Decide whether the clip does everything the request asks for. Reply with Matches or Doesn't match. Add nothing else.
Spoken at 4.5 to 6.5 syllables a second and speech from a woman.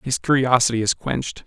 Doesn't match